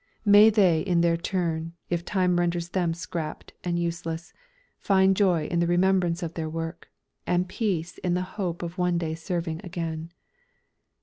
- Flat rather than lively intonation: Yes, narrow, 1.7 semitones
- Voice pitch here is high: No, medium, 175 Hz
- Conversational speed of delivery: Yes, average, 165 wpm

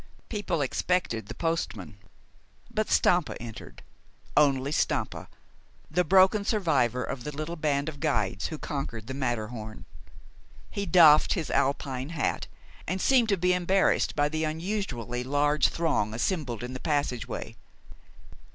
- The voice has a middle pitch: Yes, medium, 150 Hz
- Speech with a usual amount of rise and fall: No, wide, 5.7 semitones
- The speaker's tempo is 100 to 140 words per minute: Yes, slow, 135 wpm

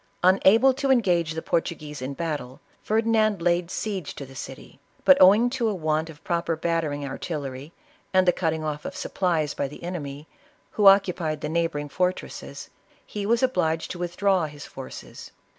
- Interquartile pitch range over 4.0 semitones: Yes, average, 4.5 semitones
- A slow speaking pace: No, average, 175 wpm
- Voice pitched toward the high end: No, medium, 170 Hz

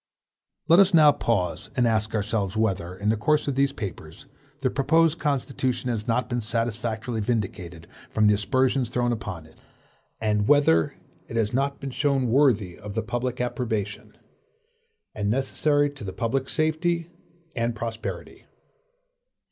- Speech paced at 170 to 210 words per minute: No, average, 155 wpm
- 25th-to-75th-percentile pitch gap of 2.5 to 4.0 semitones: No, average, 4.6 semitones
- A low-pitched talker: Yes, low, 115 Hz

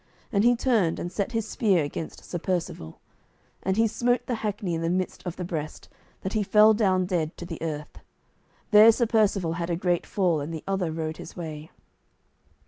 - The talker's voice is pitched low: No, medium, 185 Hz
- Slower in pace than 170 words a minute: No, average, 200 wpm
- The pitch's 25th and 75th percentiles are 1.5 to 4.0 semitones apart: No, average, 4.4 semitones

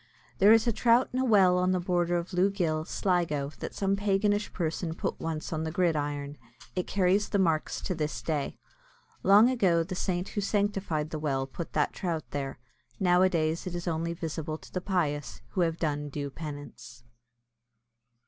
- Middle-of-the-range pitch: Yes, medium, 175 Hz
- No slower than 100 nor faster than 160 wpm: No, average, 180 wpm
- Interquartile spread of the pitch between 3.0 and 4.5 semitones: Yes, average, 3.6 semitones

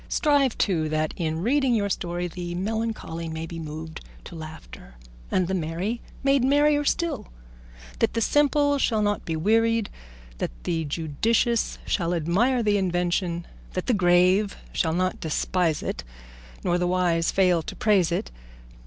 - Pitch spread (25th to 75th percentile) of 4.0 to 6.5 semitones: Yes, wide, 5.4 semitones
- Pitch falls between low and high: Yes, medium, 180 Hz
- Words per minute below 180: Yes, average, 155 wpm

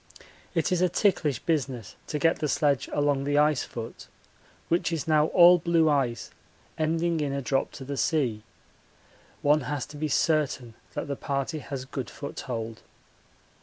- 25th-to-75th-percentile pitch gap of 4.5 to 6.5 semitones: No, average, 3.0 semitones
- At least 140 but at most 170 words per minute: Yes, average, 165 wpm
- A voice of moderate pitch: Yes, medium, 145 Hz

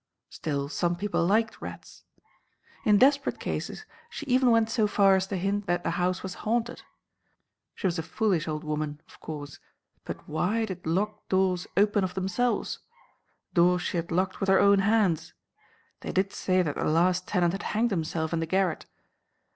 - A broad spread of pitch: No, average, 3.5 semitones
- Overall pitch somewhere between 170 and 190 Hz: Yes, medium, 185 Hz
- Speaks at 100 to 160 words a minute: No, average, 180 wpm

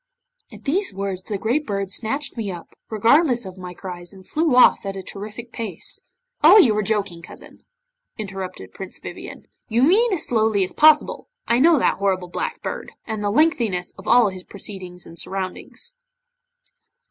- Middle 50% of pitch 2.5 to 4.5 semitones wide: No, wide, 5.4 semitones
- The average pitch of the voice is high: Yes, high, 210 Hz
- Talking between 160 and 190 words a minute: Yes, average, 175 wpm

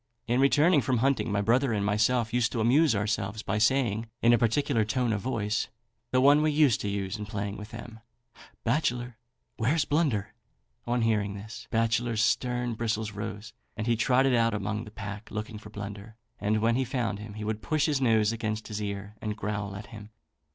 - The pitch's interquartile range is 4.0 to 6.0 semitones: No, average, 2.8 semitones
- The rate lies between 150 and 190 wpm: No, average, 200 wpm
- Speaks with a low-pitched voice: Yes, low, 110 Hz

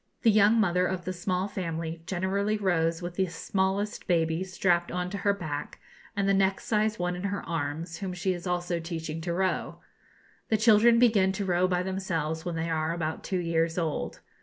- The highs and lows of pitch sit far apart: No, average, 2.8 semitones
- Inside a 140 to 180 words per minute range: No, average, 195 wpm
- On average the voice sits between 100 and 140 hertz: No, medium, 180 Hz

